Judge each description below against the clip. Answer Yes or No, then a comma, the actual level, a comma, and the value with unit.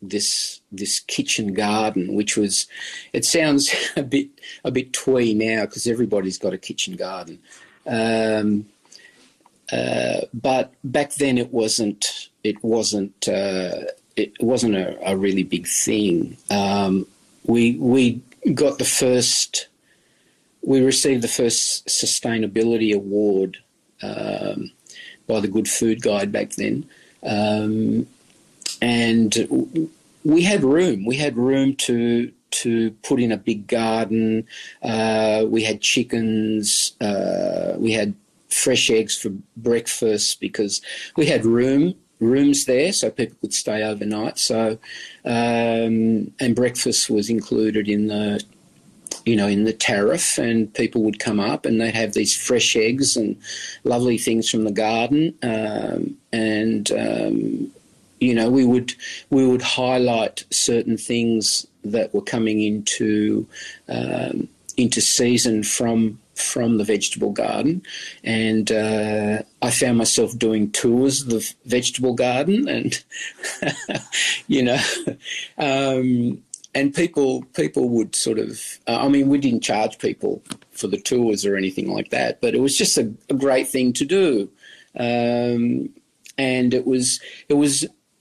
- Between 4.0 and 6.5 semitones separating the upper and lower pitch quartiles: No, average, 2.8 semitones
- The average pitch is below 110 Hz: No, low, 115 Hz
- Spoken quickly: No, slow, 135 wpm